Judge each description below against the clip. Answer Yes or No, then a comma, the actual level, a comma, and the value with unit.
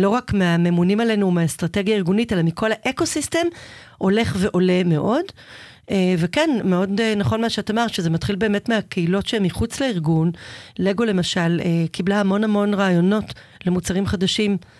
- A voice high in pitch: Yes, high, 195 Hz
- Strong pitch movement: No, average, 3.7 semitones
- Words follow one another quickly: No, average, 135 wpm